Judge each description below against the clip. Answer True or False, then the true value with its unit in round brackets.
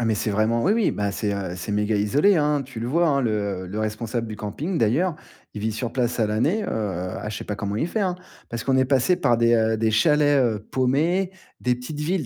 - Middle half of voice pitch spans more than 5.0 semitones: True (5.6 semitones)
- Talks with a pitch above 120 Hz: False (115 Hz)